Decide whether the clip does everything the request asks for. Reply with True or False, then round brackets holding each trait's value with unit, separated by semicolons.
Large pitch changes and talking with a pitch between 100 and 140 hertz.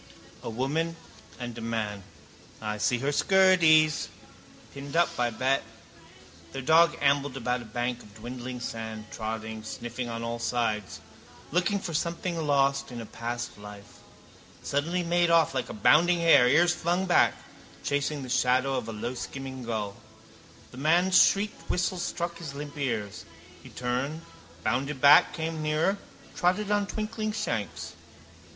True (6.1 semitones; 135 Hz)